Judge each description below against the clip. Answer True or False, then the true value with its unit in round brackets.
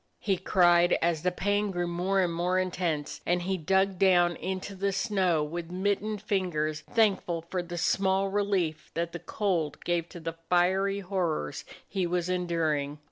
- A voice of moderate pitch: True (180 Hz)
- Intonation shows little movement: True (2.2 semitones)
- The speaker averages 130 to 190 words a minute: True (175 wpm)